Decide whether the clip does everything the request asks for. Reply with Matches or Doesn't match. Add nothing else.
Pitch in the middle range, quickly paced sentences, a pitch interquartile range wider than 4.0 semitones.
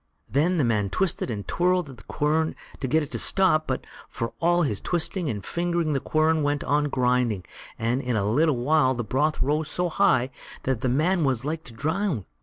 Matches